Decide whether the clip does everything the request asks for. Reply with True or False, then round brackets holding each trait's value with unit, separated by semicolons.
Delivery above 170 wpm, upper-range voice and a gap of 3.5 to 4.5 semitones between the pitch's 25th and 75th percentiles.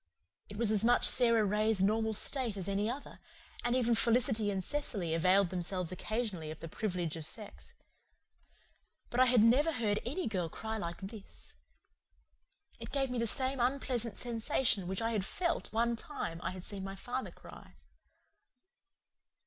False (165 wpm; 220 Hz; 4.1 semitones)